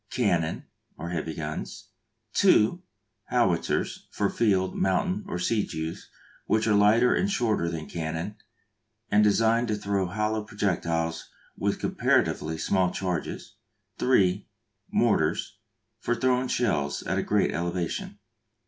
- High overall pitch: No, low, 100 Hz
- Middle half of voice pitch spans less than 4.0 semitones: No, average, 4.8 semitones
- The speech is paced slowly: Yes, slow, 120 wpm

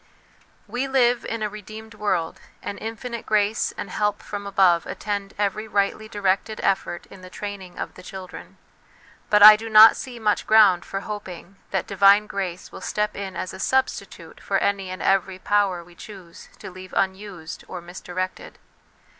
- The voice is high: Yes, high, 200 Hz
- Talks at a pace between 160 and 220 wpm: Yes, average, 170 wpm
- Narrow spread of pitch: Yes, narrow, 2.3 semitones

